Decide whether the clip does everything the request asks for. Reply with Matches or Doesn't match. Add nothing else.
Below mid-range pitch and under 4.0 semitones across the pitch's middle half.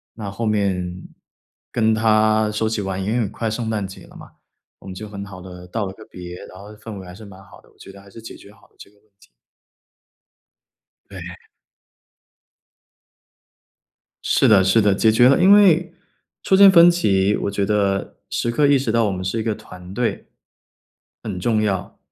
Matches